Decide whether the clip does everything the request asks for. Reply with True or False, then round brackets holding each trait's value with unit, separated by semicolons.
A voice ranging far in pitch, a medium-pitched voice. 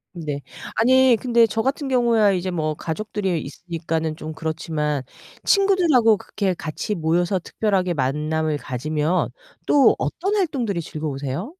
True (6.8 semitones; 175 Hz)